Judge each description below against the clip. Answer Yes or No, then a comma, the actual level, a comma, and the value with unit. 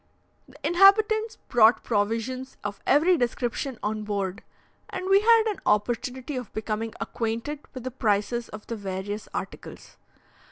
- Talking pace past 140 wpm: No, slow, 135 wpm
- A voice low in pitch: No, high, 240 Hz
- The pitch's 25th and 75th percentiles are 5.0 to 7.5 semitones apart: Yes, wide, 5.6 semitones